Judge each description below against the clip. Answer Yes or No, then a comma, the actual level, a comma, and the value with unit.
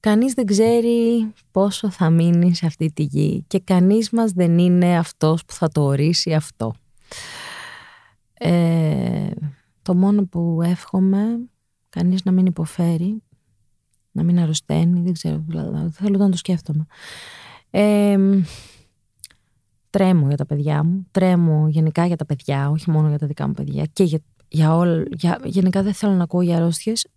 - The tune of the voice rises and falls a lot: No, average, 4.1 semitones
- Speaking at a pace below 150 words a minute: No, average, 155 wpm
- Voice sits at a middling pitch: Yes, medium, 170 Hz